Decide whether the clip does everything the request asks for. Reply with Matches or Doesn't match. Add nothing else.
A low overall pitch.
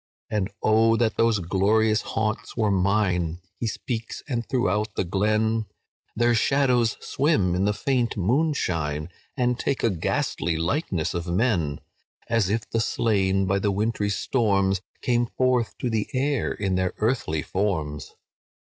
Matches